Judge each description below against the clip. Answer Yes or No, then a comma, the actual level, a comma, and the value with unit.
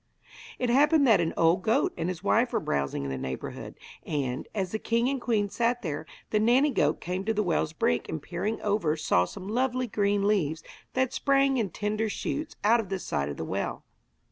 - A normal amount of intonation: No, wide, 6.6 semitones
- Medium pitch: No, high, 205 Hz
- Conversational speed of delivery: No, fast, 210 wpm